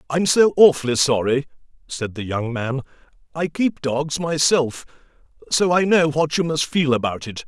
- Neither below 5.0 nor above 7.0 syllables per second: No, 4.6 syllables/s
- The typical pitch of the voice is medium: Yes, medium, 145 Hz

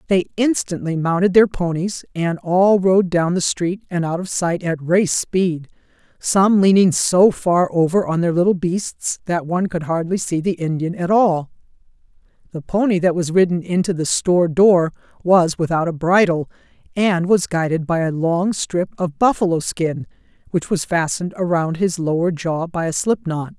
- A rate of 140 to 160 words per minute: No, average, 175 wpm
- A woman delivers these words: Yes, female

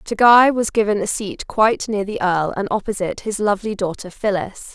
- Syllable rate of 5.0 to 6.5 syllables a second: Yes, 5.5 syllables/s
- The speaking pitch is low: No, high, 205 Hz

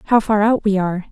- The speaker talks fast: Yes, fast, 270 wpm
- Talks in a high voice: Yes, high, 205 Hz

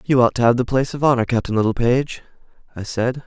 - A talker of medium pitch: No, low, 120 Hz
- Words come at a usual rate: No, fast, 220 wpm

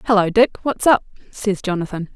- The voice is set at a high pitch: Yes, high, 205 Hz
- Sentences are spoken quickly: No, average, 165 wpm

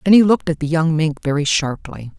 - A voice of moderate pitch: Yes, medium, 160 Hz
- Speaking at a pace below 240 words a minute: No, fast, 245 wpm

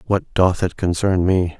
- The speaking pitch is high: No, very low, 95 Hz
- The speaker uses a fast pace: No, average, 190 wpm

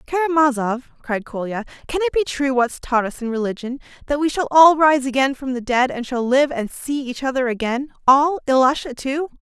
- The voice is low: No, very high, 270 Hz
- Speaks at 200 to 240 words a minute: Yes, fast, 205 wpm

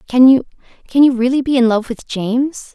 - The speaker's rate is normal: Yes, average, 195 wpm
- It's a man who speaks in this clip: No, female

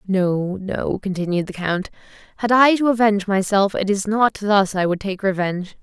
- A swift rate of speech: No, average, 185 wpm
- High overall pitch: Yes, high, 200 Hz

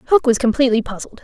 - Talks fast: No, average, 195 wpm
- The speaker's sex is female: Yes, female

